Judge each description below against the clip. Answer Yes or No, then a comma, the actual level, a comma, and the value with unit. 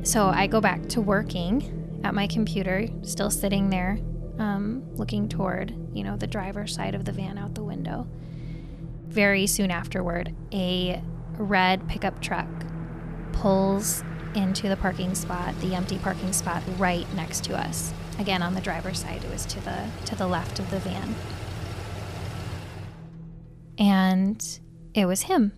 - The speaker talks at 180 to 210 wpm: No, average, 150 wpm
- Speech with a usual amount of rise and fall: Yes, average, 3.8 semitones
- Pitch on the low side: No, medium, 175 Hz